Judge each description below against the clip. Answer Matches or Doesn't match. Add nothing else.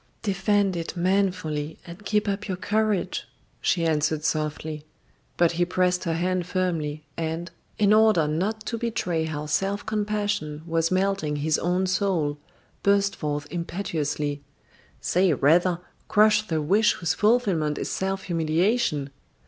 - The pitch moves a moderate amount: Matches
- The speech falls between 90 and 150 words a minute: Matches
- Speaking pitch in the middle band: Matches